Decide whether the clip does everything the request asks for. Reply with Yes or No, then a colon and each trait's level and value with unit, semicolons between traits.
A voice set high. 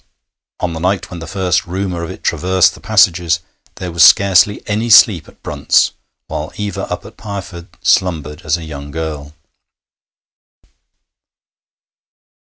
No: very low, 90 Hz